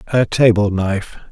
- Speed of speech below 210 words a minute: Yes, slow, 135 wpm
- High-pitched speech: No, low, 105 Hz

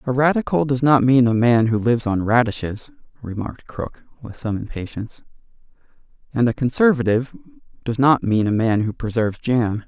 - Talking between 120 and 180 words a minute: Yes, average, 165 wpm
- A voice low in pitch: Yes, low, 120 Hz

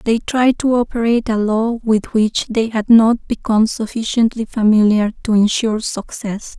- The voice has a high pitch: Yes, high, 225 Hz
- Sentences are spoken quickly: No, average, 155 wpm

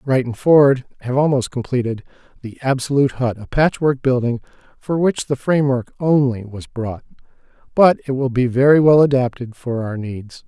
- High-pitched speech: No, low, 130 Hz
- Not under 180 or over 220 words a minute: No, average, 160 wpm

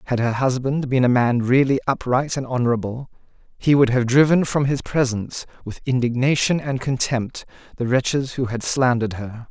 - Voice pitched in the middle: No, low, 125 Hz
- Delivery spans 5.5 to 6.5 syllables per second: No, 5.3 syllables/s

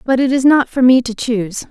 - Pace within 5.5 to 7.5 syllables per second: Yes, 5.6 syllables/s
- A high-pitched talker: Yes, very high, 250 Hz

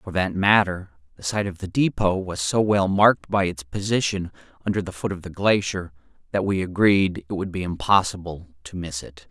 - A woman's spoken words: No, male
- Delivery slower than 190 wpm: No, average, 200 wpm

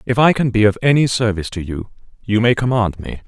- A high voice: No, low, 110 Hz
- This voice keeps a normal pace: No, fast, 240 wpm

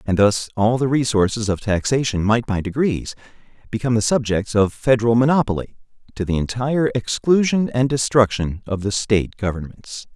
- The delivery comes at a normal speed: Yes, average, 155 wpm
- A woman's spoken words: No, male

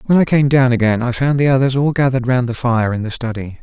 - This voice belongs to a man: Yes, male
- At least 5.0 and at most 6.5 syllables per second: Yes, 6.4 syllables/s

